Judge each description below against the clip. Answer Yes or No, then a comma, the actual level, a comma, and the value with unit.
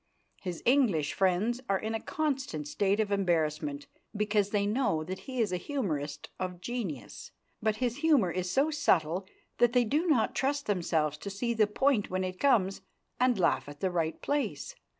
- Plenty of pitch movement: Yes, wide, 5.8 semitones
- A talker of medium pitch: No, high, 200 Hz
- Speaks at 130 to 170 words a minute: No, average, 180 wpm